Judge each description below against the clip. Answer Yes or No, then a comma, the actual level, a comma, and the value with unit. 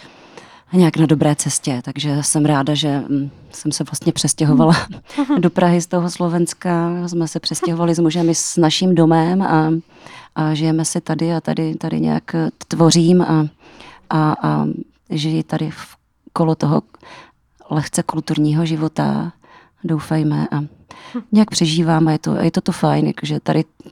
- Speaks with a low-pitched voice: No, medium, 160 Hz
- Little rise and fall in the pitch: Yes, narrow, 2.1 semitones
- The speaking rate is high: No, average, 150 wpm